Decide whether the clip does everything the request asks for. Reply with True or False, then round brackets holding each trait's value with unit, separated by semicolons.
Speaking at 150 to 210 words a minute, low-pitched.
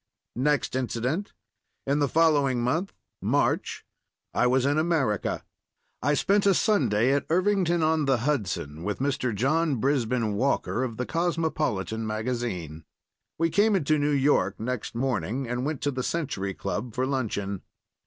False (140 wpm; 130 Hz)